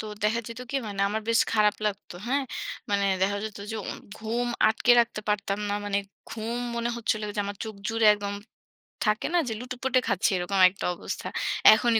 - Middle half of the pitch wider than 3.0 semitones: No, narrow, 2.5 semitones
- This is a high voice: Yes, high, 220 Hz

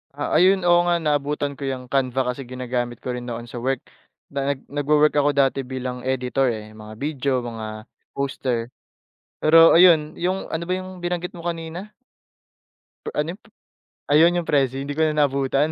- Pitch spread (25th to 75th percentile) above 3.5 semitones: Yes, average, 4.0 semitones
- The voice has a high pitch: No, medium, 140 Hz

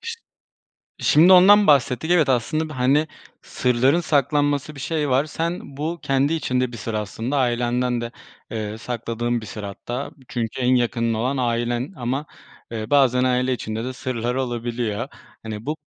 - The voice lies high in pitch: No, low, 125 Hz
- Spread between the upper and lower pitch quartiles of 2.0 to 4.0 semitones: Yes, average, 3.5 semitones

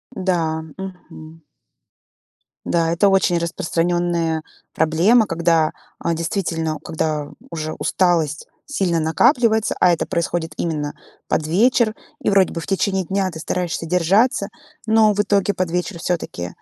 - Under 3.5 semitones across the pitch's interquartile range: Yes, average, 3.1 semitones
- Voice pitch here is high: No, medium, 175 Hz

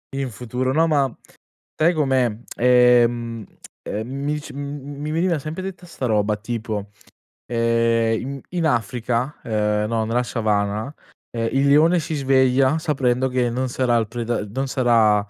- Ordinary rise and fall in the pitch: Yes, average, 3.4 semitones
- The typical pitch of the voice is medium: No, low, 125 Hz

